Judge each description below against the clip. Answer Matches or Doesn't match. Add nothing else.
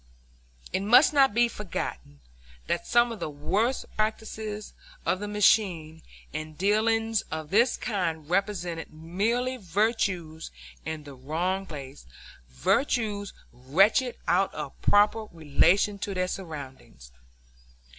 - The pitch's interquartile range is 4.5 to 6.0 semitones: Matches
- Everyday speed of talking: Doesn't match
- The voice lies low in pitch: Doesn't match